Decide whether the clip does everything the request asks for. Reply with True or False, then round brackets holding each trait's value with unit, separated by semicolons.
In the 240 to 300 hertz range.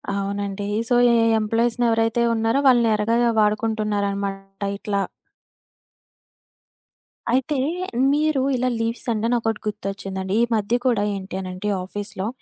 False (210 Hz)